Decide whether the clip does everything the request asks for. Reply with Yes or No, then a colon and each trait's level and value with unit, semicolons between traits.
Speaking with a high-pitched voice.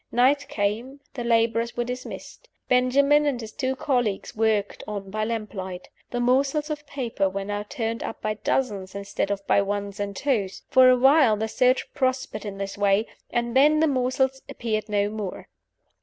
Yes: high, 230 Hz